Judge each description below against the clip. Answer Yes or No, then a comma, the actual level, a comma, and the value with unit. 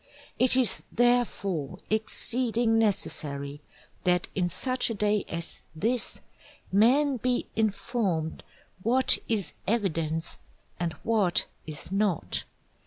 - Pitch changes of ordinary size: No, wide, 5.7 semitones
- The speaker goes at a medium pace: No, slow, 105 wpm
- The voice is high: Yes, high, 210 Hz